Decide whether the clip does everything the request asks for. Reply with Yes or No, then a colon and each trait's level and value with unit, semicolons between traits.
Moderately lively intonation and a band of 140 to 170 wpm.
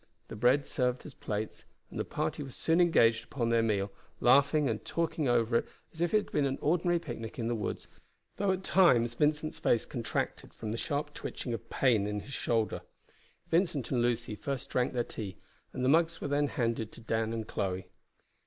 No: average, 4.7 semitones; average, 200 wpm